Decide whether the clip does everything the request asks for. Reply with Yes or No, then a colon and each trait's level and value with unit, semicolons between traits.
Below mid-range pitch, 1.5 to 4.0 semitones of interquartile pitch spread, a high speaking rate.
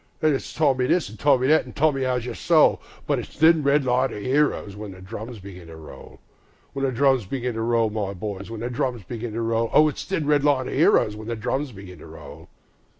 No: low, 120 Hz; average, 4.6 semitones; fast, 230 wpm